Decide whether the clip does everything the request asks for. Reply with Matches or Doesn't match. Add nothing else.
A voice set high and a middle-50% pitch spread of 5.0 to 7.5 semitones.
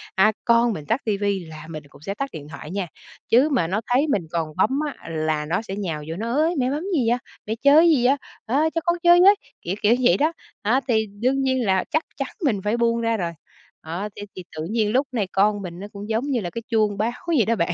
Matches